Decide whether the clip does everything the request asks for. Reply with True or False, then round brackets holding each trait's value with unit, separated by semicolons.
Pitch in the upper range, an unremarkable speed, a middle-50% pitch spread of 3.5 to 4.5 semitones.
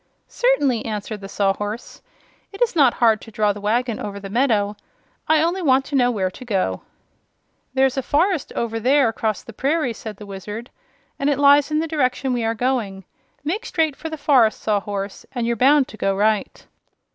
False (240 Hz; 190 wpm; 5.3 semitones)